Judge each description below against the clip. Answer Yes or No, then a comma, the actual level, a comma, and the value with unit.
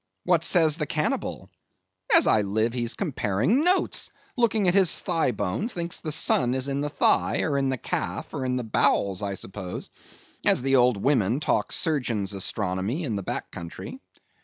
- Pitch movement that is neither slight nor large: No, wide, 7.6 semitones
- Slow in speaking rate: No, average, 180 wpm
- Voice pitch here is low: Yes, low, 130 Hz